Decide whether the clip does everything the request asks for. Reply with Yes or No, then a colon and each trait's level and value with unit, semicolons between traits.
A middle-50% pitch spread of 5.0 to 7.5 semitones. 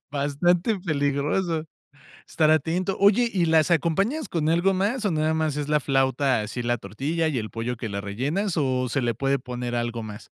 Yes: wide, 5.5 semitones